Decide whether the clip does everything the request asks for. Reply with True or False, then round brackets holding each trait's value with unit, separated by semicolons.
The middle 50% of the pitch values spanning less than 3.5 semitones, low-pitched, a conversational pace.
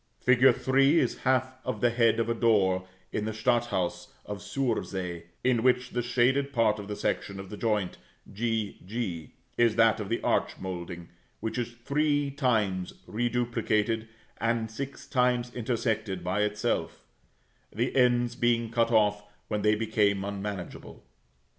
True (2.9 semitones; 115 Hz; 150 wpm)